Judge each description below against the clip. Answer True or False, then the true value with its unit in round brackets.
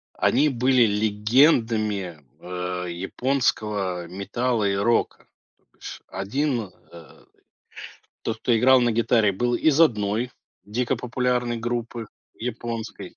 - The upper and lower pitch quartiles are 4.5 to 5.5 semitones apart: False (3.4 semitones)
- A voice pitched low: True (115 Hz)